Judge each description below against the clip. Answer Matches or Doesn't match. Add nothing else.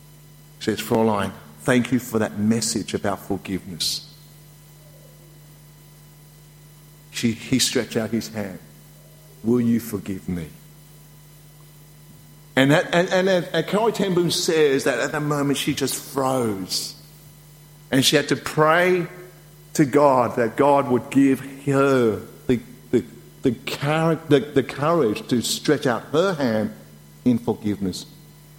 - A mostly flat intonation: Doesn't match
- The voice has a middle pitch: Matches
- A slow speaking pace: Matches